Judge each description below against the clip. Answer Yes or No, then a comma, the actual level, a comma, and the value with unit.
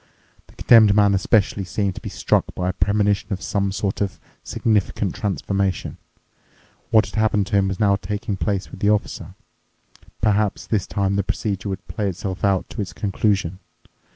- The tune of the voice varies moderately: No, narrow, 1.4 semitones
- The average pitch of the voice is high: No, low, 100 Hz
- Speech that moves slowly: No, average, 175 wpm